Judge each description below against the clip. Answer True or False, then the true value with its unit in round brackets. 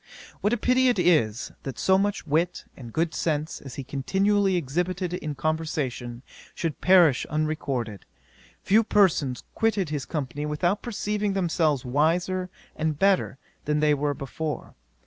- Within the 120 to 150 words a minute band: True (140 wpm)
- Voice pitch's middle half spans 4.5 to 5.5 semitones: True (4.9 semitones)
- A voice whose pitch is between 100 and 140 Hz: False (160 Hz)